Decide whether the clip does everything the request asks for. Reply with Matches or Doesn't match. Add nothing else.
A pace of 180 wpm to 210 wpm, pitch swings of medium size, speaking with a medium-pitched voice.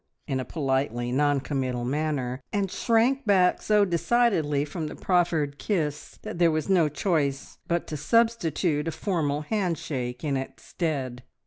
Doesn't match